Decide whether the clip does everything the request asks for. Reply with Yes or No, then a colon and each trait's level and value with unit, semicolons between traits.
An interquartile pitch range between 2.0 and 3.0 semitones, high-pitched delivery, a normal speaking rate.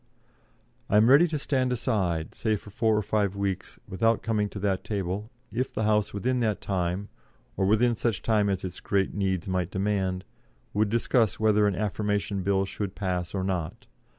No: narrow, 2.4 semitones; low, 100 Hz; average, 180 wpm